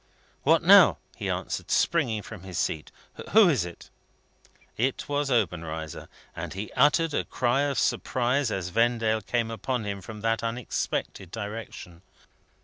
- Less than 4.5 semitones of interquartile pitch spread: No, average, 4.8 semitones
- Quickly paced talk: No, average, 140 wpm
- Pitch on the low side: Yes, low, 115 Hz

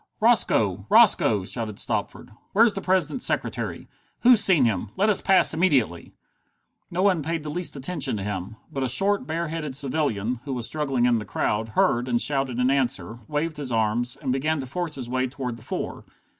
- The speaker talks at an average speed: Yes, average, 190 wpm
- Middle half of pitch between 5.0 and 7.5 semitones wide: Yes, wide, 5.5 semitones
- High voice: No, low, 135 Hz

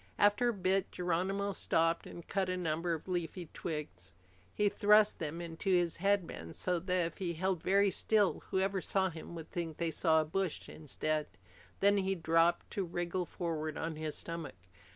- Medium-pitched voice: Yes, medium, 175 Hz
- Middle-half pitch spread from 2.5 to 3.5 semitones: Yes, average, 2.9 semitones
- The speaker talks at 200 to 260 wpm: No, average, 175 wpm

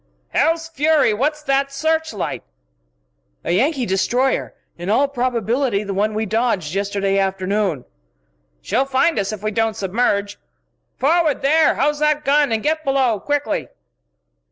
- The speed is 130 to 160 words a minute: Yes, average, 140 wpm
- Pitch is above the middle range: Yes, high, 245 Hz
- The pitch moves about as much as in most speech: No, wide, 6.2 semitones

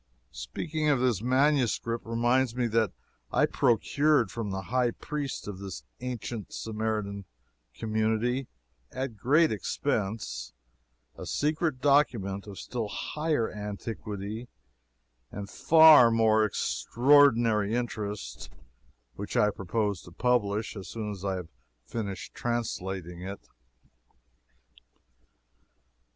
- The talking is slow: Yes, slow, 105 wpm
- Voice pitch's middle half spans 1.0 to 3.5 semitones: No, average, 3.9 semitones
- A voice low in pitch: Yes, low, 110 Hz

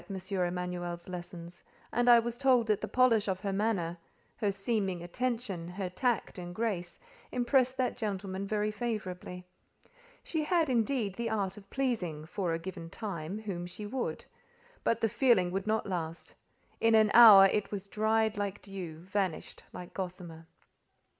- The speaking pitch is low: No, high, 200 Hz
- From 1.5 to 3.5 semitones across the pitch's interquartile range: No, average, 4.1 semitones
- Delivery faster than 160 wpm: No, average, 155 wpm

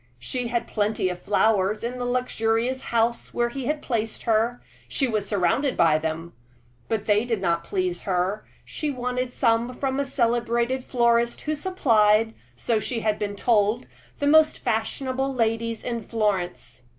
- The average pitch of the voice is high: Yes, high, 230 Hz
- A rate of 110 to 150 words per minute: No, average, 160 wpm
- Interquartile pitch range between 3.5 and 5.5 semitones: No, average, 3.1 semitones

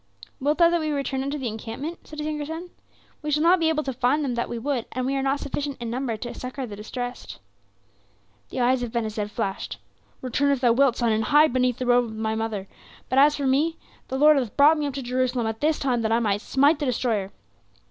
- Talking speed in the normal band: No, fast, 250 wpm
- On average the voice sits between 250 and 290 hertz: Yes, very high, 260 Hz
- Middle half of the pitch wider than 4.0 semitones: No, average, 3.6 semitones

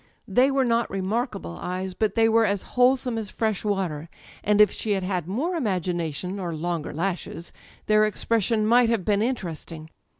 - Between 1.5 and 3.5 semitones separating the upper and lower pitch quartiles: No, average, 4.1 semitones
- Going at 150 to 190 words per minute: Yes, average, 180 wpm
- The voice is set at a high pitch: Yes, high, 205 Hz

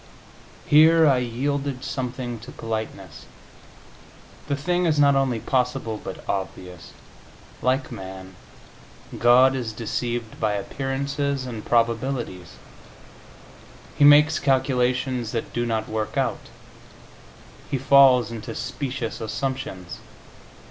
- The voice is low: Yes, low, 125 Hz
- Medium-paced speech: No, slow, 105 wpm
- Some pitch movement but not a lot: Yes, average, 3.5 semitones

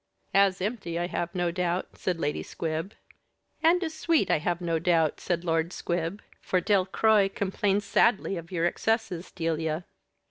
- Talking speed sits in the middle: Yes, average, 165 wpm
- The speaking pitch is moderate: Yes, medium, 180 Hz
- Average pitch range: Yes, average, 3.1 semitones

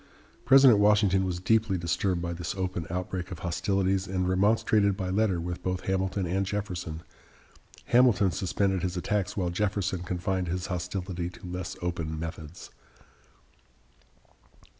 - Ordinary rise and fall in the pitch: No, narrow, 2.0 semitones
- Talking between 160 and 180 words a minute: No, slow, 135 wpm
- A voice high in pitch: No, very low, 95 Hz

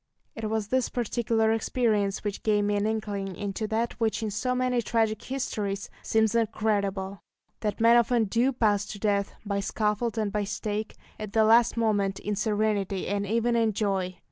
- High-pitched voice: Yes, high, 215 Hz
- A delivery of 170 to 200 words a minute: Yes, average, 175 wpm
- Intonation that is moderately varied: No, narrow, 2.1 semitones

